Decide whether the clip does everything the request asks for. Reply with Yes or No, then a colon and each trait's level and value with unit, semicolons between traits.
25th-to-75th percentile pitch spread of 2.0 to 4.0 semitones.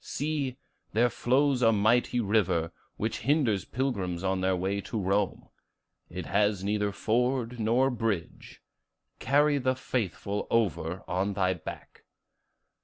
No: average, 4.5 semitones